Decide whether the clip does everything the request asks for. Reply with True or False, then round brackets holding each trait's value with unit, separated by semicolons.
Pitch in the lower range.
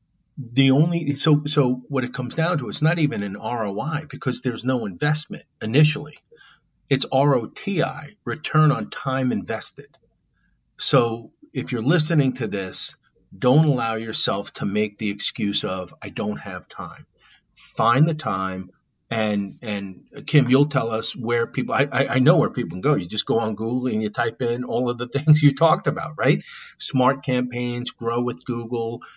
True (125 Hz)